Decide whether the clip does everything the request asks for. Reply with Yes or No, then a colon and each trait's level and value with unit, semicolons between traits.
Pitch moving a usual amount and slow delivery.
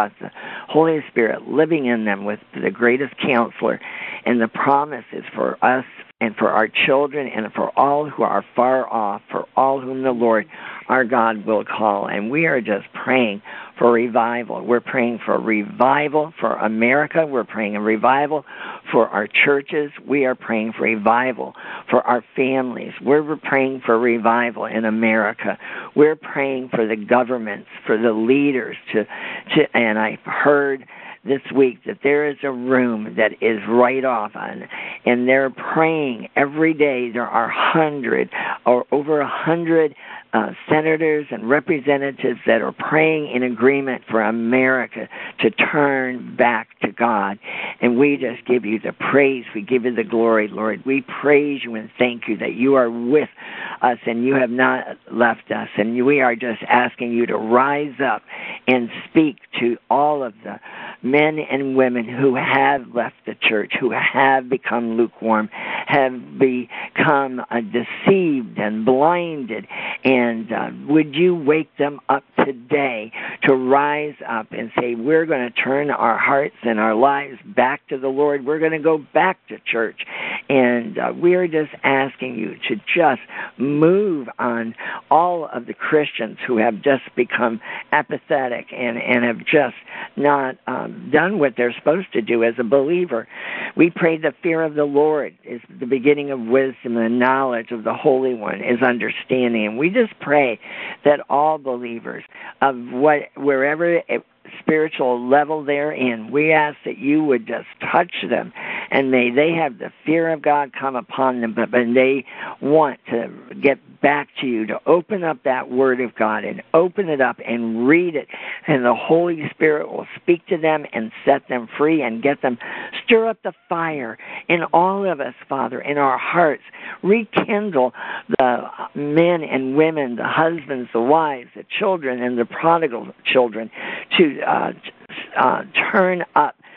No: average, 3.8 semitones; average, 165 wpm